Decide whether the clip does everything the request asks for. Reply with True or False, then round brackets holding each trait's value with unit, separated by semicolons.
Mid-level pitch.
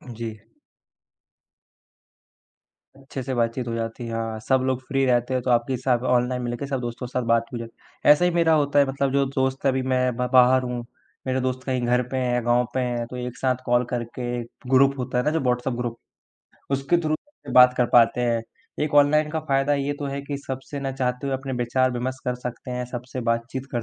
False (125 Hz)